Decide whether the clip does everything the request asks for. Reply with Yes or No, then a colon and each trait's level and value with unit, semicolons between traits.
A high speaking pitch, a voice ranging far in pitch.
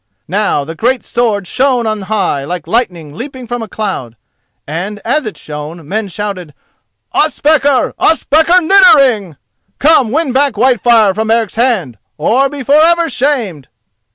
Yes: high, 225 Hz; wide, 6.6 semitones